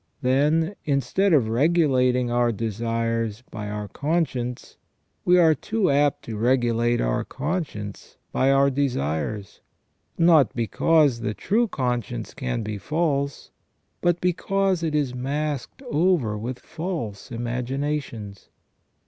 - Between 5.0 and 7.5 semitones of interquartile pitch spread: Yes, average, 5.3 semitones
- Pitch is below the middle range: Yes, low, 130 Hz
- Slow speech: Yes, slow, 120 wpm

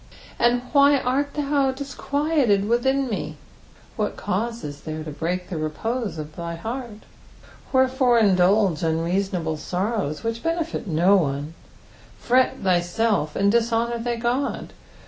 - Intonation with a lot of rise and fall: Yes, wide, 6.7 semitones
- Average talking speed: No, slow, 130 wpm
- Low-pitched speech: No, high, 220 Hz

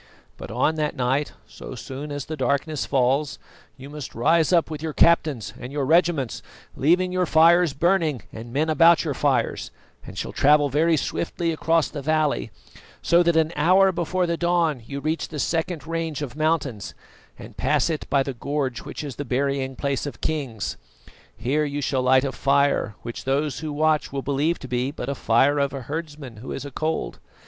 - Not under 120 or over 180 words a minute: No, average, 190 wpm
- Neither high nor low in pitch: Yes, medium, 145 Hz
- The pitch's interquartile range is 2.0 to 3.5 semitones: Yes, average, 3.0 semitones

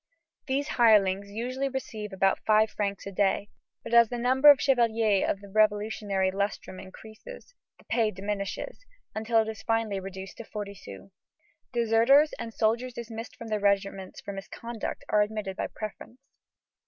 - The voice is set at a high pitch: Yes, high, 215 Hz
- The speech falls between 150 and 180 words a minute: Yes, average, 160 wpm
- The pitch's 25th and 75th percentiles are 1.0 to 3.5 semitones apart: Yes, average, 2.8 semitones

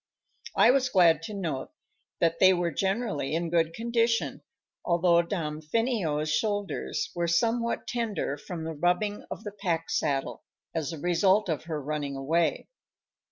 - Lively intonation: No, average, 4.6 semitones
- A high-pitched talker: No, medium, 170 Hz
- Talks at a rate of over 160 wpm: No, average, 145 wpm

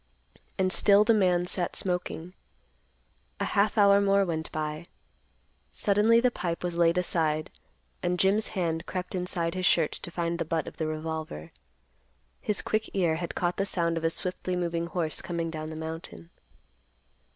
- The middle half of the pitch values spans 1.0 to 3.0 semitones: Yes, narrow, 2.6 semitones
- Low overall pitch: No, medium, 175 Hz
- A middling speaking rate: Yes, average, 165 wpm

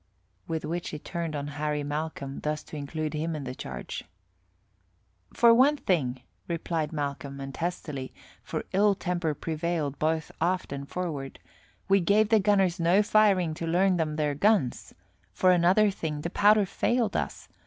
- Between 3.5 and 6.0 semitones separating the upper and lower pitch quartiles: Yes, average, 4.2 semitones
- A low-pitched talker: No, medium, 165 Hz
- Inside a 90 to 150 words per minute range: No, average, 160 wpm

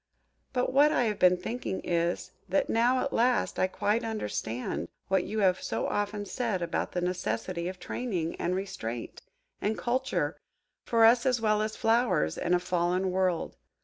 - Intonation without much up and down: No, average, 4.5 semitones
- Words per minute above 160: Yes, average, 175 wpm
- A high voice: Yes, high, 200 Hz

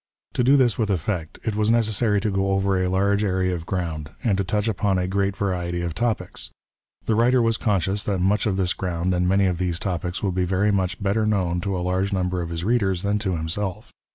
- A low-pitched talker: Yes, very low, 95 Hz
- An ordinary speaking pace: No, fast, 235 wpm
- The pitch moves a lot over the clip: No, narrow, 2.5 semitones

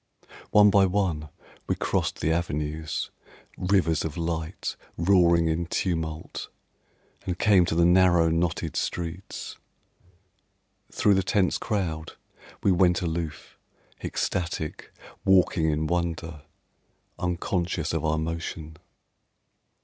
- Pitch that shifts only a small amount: Yes, narrow, 2.2 semitones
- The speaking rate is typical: No, slow, 105 wpm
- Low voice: Yes, very low, 85 Hz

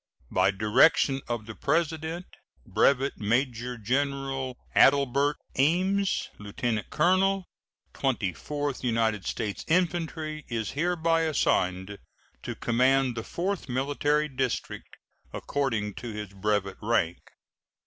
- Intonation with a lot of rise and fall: Yes, wide, 5.7 semitones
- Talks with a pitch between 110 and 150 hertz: Yes, low, 135 Hz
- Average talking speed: No, slow, 105 wpm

